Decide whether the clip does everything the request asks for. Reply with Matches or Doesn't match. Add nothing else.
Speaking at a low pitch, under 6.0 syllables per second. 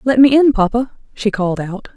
Doesn't match